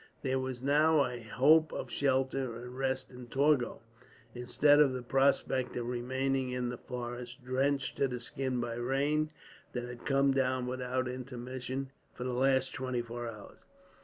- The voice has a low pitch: Yes, low, 130 Hz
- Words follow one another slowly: No, average, 165 wpm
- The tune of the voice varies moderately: No, narrow, 1.7 semitones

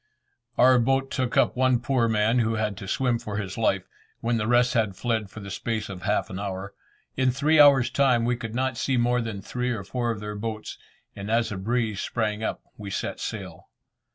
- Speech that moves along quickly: Yes, fast, 215 wpm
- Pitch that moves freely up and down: No, average, 2.8 semitones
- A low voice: Yes, low, 115 Hz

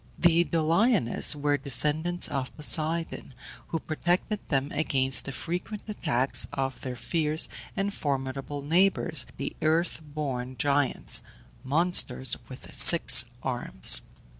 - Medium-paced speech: No, slow, 115 wpm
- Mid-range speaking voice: Yes, medium, 150 Hz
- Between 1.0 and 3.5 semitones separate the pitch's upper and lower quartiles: No, average, 4.1 semitones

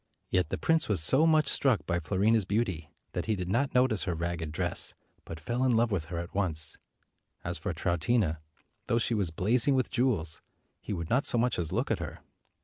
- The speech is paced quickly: Yes, fast, 215 wpm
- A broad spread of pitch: Yes, wide, 6.3 semitones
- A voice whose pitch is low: Yes, low, 100 Hz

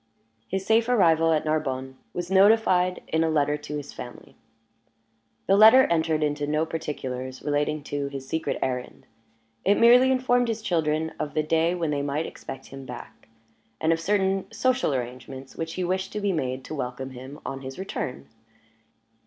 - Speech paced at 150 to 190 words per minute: Yes, average, 170 wpm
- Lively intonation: Yes, wide, 5.7 semitones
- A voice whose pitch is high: No, medium, 155 Hz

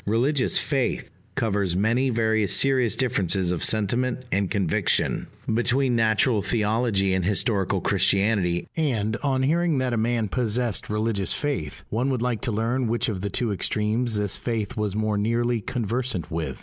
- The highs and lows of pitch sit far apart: No, average, 3.5 semitones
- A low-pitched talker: Yes, low, 110 Hz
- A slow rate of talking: No, average, 155 wpm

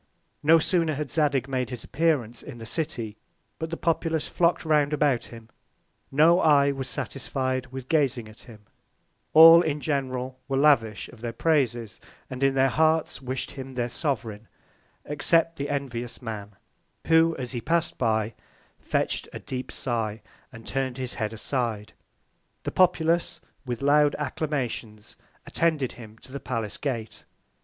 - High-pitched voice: No, low, 135 Hz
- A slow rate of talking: No, average, 150 wpm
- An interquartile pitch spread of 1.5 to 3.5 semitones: No, average, 4.3 semitones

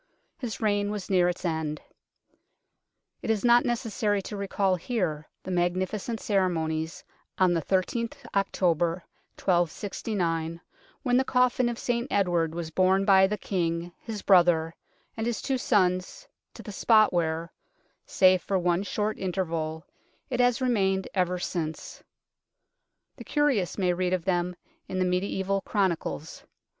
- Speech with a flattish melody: No, average, 3.3 semitones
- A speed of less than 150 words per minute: Yes, average, 140 wpm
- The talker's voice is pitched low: No, medium, 185 Hz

